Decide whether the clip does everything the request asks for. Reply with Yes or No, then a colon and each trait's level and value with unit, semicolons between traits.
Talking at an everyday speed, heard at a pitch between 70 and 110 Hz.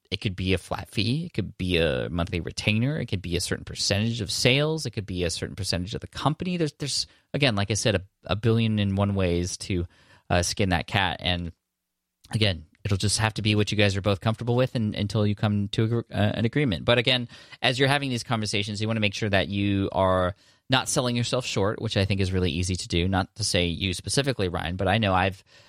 No: fast, 250 wpm; low, 105 Hz